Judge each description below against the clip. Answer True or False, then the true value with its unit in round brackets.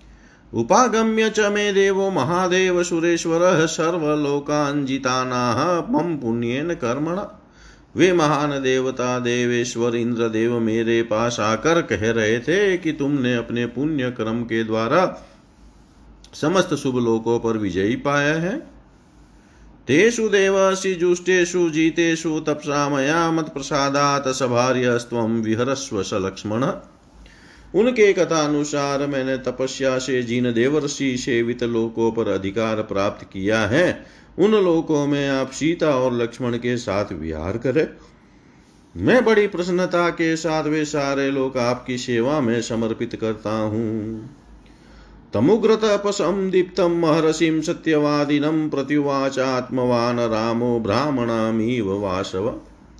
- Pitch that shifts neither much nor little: False (5.7 semitones)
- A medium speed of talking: False (105 wpm)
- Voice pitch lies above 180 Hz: False (135 Hz)